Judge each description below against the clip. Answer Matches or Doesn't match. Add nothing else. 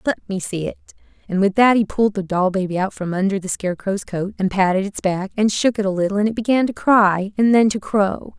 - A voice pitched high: Matches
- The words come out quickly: Matches